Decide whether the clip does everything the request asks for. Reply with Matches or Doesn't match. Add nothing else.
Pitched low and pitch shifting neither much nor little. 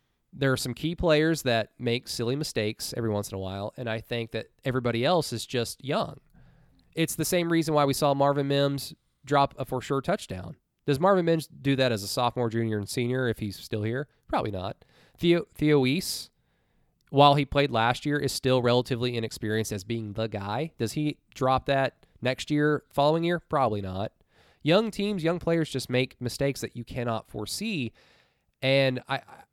Matches